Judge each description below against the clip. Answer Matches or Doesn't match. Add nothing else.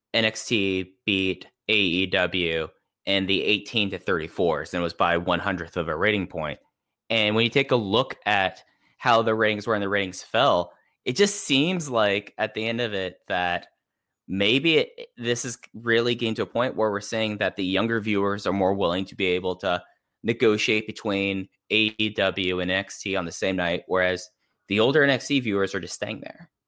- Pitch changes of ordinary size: Matches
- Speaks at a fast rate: Doesn't match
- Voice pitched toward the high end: Doesn't match